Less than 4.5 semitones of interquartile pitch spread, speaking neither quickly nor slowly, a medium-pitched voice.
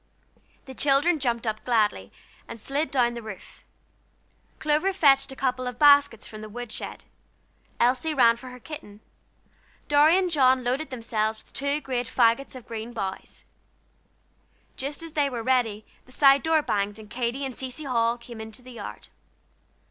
No: average, 3.5 semitones; average, 165 wpm; very high, 250 Hz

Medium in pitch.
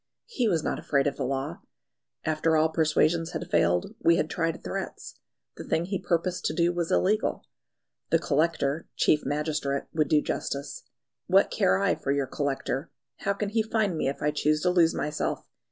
Yes: medium, 155 Hz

